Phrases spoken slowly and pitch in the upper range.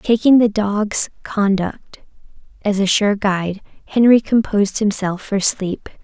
Yes: slow, 130 wpm; high, 205 Hz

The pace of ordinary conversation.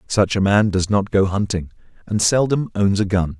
No: fast, 210 wpm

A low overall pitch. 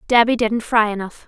No: high, 225 Hz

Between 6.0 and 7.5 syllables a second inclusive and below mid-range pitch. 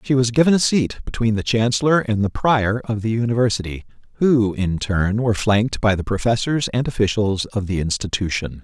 No: 5.4 syllables/s; low, 110 Hz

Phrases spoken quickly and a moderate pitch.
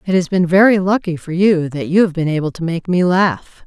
Yes: fast, 260 wpm; medium, 175 Hz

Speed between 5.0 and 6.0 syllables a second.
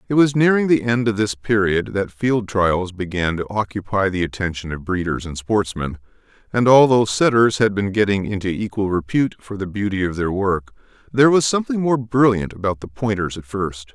Yes: 5.4 syllables/s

